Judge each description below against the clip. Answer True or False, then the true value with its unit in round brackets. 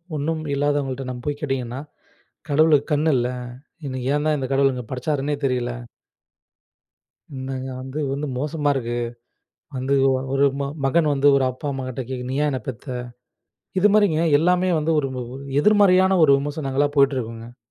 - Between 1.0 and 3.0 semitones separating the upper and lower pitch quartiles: True (2.5 semitones)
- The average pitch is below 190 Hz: True (140 Hz)